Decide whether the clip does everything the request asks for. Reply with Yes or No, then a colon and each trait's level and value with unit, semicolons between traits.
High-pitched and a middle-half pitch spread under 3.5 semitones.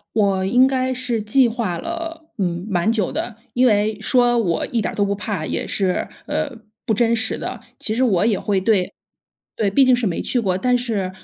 No: high, 220 Hz; average, 4.0 semitones